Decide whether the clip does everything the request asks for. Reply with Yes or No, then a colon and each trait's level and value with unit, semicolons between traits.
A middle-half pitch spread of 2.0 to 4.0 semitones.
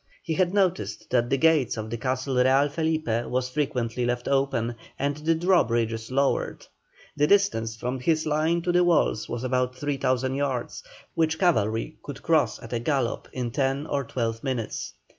No: average, 4.4 semitones